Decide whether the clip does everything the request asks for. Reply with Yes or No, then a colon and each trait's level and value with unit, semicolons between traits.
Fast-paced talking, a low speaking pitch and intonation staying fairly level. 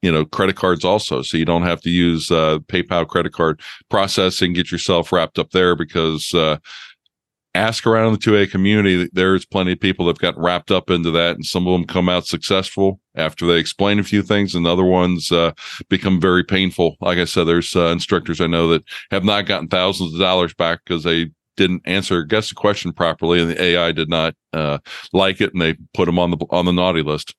Yes: fast, 225 wpm; very low, 90 Hz; narrow, 2.1 semitones